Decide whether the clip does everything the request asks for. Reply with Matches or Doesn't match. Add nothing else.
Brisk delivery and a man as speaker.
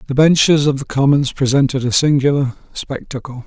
Doesn't match